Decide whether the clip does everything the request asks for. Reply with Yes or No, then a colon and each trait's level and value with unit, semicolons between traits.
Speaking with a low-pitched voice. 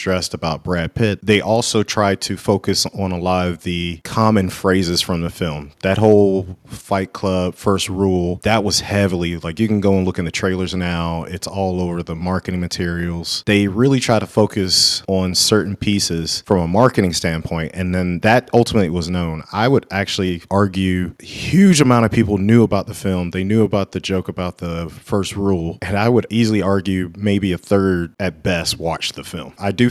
Yes: very low, 95 Hz